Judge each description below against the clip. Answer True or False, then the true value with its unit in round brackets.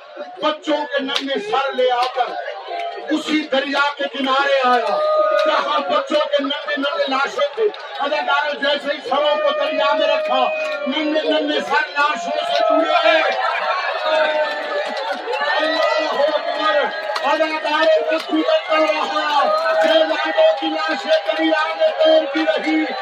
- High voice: True (295 Hz)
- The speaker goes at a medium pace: False (95 wpm)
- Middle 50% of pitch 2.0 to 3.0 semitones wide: True (2.4 semitones)